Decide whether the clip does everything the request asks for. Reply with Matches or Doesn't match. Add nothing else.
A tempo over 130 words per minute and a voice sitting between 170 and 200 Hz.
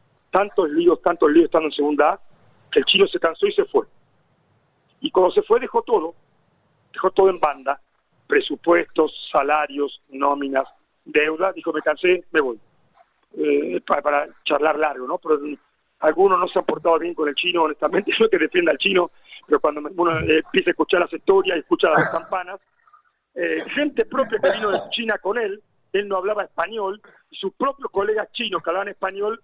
Matches